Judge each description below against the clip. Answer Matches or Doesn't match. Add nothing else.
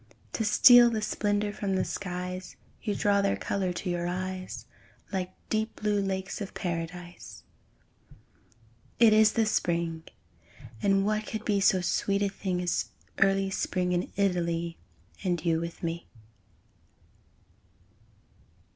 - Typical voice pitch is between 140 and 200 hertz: Matches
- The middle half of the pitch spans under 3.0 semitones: Matches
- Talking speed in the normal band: Doesn't match